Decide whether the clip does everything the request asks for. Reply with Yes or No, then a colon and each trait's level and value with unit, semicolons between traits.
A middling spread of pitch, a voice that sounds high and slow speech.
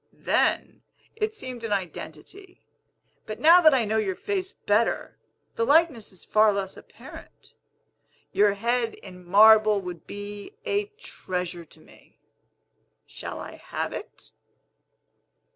No: wide, 6.3 semitones; high, 215 Hz; slow, 125 wpm